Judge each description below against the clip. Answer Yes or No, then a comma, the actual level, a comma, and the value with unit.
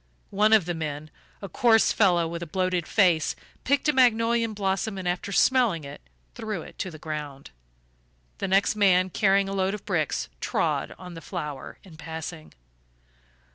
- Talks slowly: No, average, 170 wpm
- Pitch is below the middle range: No, medium, 185 Hz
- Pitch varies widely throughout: No, average, 4.4 semitones